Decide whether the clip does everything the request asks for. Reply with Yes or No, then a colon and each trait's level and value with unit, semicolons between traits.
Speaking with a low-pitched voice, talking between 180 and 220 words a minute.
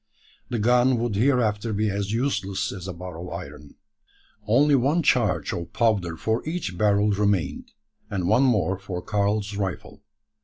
No: low, 105 Hz; average, 155 wpm